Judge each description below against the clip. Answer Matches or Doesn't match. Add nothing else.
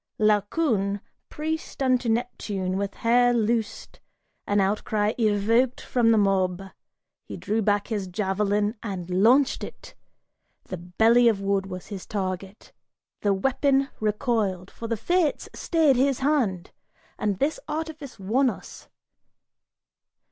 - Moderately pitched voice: Doesn't match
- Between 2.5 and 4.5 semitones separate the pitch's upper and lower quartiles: Matches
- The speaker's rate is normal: Doesn't match